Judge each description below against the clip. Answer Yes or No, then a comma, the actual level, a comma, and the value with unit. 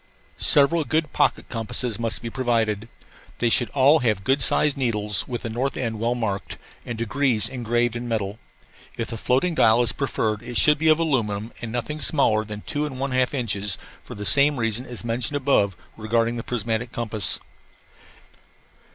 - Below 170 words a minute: No, average, 175 wpm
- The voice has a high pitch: No, low, 120 Hz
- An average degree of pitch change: Yes, average, 3.3 semitones